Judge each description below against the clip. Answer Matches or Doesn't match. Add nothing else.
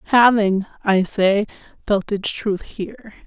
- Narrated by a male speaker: Doesn't match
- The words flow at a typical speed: Doesn't match